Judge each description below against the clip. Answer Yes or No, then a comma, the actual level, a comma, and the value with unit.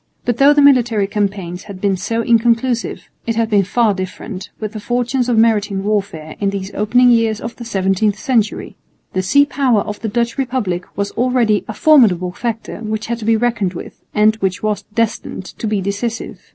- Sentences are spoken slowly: No, average, 190 wpm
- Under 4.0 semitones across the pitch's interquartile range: Yes, average, 3.0 semitones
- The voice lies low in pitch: No, high, 220 Hz